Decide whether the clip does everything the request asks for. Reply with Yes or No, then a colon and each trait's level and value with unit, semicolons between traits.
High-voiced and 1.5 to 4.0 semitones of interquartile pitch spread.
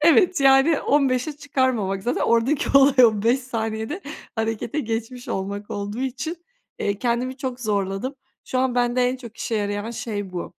Yes: high, 245 Hz; average, 3.5 semitones